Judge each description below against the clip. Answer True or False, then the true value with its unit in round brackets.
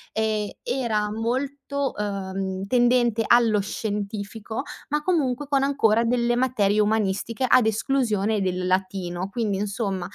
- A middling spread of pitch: True (3.7 semitones)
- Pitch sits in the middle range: False (220 Hz)